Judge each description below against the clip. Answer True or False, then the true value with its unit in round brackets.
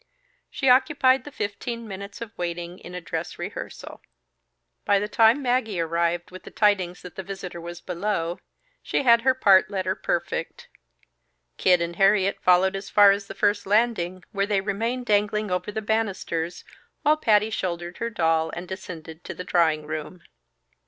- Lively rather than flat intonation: False (3.8 semitones)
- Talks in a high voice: True (195 Hz)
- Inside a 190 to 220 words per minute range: False (165 wpm)